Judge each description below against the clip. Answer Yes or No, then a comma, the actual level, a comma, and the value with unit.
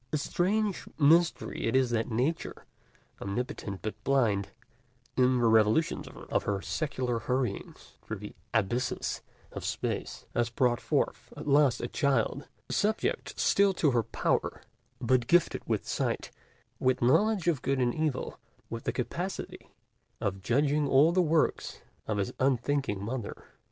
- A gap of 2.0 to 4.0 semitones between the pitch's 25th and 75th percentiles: No, average, 4.8 semitones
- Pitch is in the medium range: No, low, 130 Hz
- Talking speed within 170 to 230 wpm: No, average, 140 wpm